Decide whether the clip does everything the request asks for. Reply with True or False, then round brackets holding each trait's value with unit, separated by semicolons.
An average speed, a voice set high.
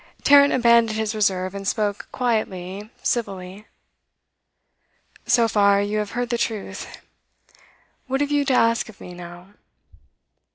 False (130 wpm; 215 Hz)